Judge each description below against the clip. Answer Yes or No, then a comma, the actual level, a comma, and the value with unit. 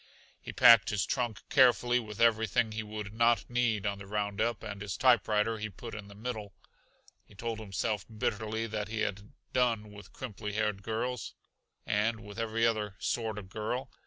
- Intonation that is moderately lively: No, narrow, 2.0 semitones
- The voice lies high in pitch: No, low, 110 Hz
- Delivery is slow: No, average, 175 wpm